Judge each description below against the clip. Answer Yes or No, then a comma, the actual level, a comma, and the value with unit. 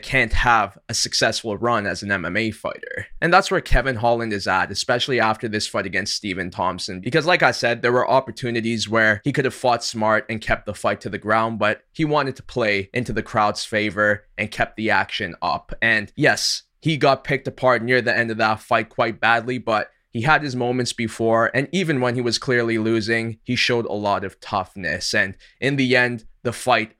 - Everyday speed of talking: No, fast, 215 wpm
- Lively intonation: No, average, 2.8 semitones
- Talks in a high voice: No, low, 115 Hz